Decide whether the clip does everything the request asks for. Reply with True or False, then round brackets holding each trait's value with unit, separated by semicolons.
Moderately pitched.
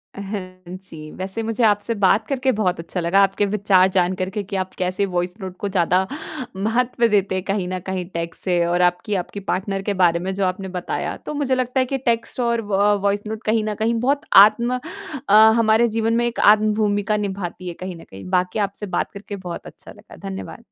False (200 Hz)